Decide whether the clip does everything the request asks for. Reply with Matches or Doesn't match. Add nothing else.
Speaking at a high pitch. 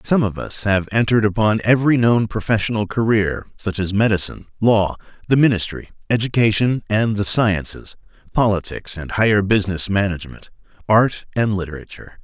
Doesn't match